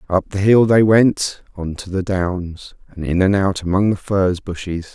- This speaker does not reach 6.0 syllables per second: Yes, 4.5 syllables/s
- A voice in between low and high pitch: No, very low, 95 Hz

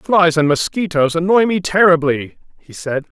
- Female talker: No, male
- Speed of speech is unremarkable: Yes, average, 170 wpm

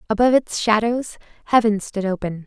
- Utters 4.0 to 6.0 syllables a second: Yes, 5.7 syllables/s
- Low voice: No, high, 215 Hz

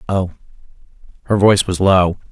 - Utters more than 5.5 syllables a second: Yes, 5.7 syllables/s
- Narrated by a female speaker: No, male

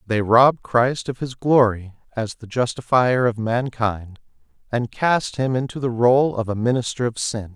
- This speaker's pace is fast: No, average, 175 wpm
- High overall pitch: No, low, 120 Hz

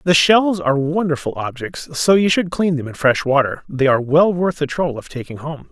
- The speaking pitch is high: No, medium, 155 Hz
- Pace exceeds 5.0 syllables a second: Yes, 5.4 syllables/s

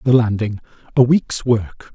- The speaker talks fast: No, average, 155 wpm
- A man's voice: Yes, male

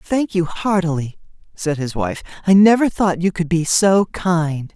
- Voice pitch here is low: No, medium, 175 Hz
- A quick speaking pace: No, average, 175 wpm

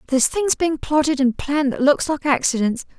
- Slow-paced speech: No, average, 200 wpm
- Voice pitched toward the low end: No, very high, 280 Hz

